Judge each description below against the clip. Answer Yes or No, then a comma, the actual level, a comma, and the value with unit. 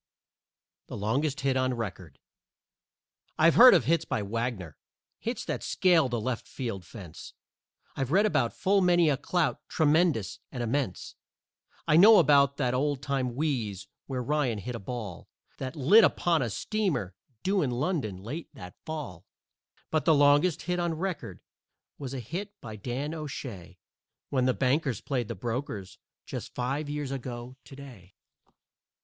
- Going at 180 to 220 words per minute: No, average, 155 wpm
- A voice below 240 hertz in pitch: Yes, low, 135 Hz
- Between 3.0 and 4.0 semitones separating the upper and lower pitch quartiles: No, average, 5.1 semitones